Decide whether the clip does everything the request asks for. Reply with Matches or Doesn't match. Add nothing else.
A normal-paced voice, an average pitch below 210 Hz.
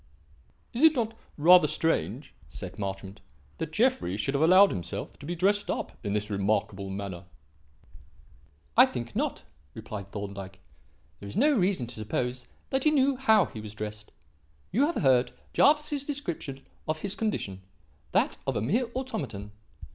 Matches